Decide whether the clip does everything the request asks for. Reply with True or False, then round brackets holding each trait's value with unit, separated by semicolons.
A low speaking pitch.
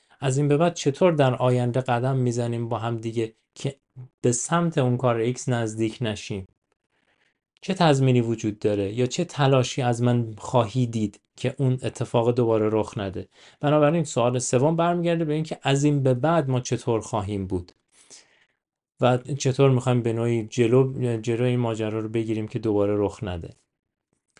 True (125 Hz)